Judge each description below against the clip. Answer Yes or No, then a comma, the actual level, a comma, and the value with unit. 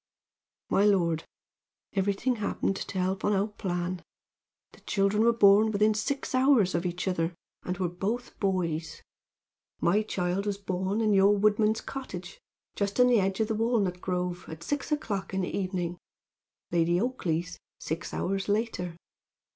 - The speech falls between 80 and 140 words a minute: No, average, 155 wpm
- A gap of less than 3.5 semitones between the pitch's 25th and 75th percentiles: Yes, average, 3.0 semitones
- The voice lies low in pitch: No, high, 195 Hz